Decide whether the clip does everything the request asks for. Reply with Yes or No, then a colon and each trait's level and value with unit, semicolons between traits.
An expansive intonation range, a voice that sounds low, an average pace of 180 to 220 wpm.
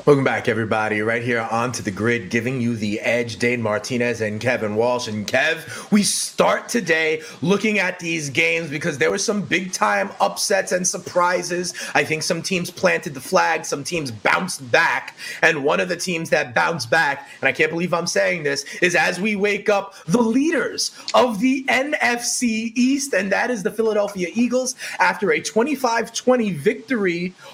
No: wide, 8.3 semitones; medium, 180 Hz; average, 185 wpm